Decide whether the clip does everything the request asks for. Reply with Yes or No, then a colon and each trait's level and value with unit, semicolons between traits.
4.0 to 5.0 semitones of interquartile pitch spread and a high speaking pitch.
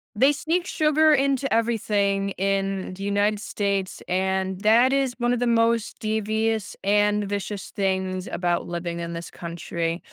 No: average, 3.5 semitones; high, 205 Hz